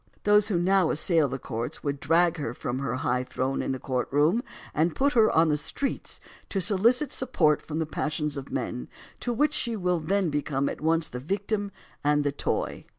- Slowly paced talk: No, average, 200 wpm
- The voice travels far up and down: Yes, wide, 6.0 semitones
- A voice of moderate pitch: Yes, medium, 160 Hz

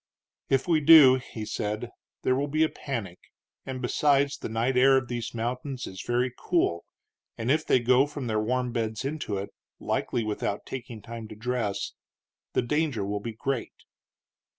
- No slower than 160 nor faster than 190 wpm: Yes, average, 175 wpm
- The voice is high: No, low, 125 Hz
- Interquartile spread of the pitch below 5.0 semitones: Yes, average, 3.5 semitones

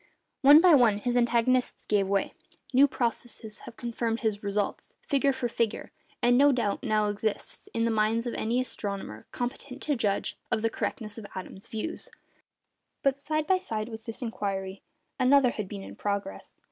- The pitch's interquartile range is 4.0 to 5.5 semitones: No, average, 3.5 semitones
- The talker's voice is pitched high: Yes, high, 230 Hz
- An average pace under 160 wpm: No, average, 170 wpm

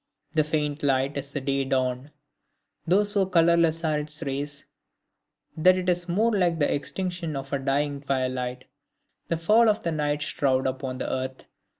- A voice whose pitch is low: No, medium, 150 Hz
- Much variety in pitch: No, average, 3.9 semitones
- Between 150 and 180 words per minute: Yes, average, 170 wpm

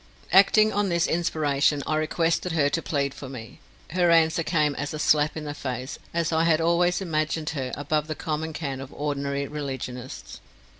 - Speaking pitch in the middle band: Yes, medium, 155 Hz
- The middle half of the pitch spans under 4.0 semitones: Yes, average, 2.8 semitones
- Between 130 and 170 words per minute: No, average, 185 wpm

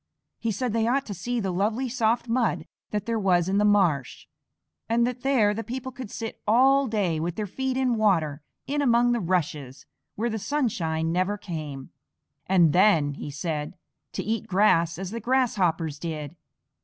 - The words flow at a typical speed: Yes, average, 180 wpm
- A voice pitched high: Yes, high, 205 Hz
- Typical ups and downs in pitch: No, wide, 6.0 semitones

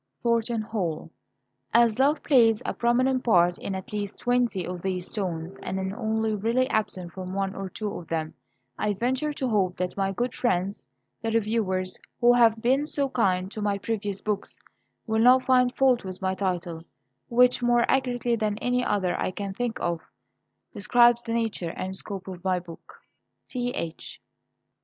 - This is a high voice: Yes, high, 215 Hz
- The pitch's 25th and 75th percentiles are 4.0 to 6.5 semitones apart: Yes, average, 4.3 semitones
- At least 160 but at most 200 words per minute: Yes, average, 170 wpm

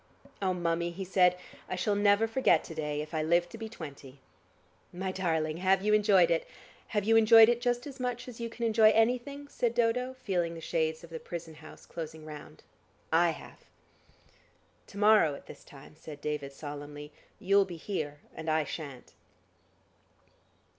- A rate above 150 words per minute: Yes, average, 175 wpm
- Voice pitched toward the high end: No, medium, 180 Hz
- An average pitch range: No, wide, 5.9 semitones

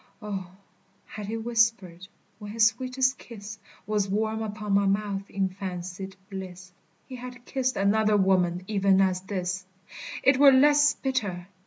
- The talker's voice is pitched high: Yes, high, 205 Hz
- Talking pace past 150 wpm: No, average, 145 wpm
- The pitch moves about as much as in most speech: Yes, average, 3.2 semitones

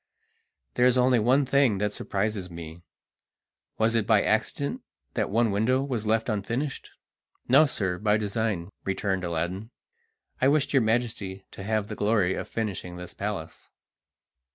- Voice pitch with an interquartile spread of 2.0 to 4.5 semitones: Yes, average, 4.1 semitones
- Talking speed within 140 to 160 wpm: Yes, average, 150 wpm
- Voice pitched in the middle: No, low, 110 Hz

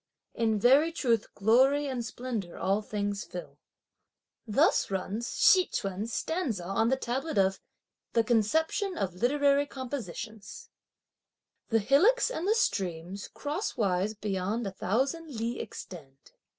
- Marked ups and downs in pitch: Yes, wide, 6.2 semitones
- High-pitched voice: Yes, high, 230 Hz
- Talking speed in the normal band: No, slow, 125 wpm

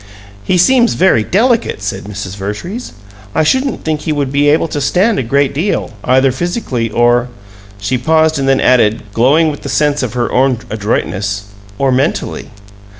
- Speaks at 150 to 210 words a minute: Yes, average, 175 wpm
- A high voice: No, low, 135 Hz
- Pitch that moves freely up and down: Yes, wide, 5.8 semitones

